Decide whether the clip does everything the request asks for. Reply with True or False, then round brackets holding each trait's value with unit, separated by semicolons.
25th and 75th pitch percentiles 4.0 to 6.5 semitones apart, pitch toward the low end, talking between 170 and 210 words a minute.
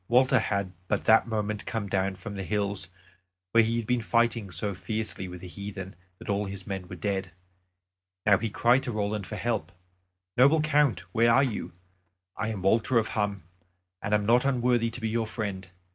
False (3.1 semitones; 105 Hz; 190 wpm)